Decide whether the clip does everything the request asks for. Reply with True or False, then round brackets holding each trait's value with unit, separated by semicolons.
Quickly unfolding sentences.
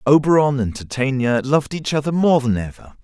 False (180 wpm)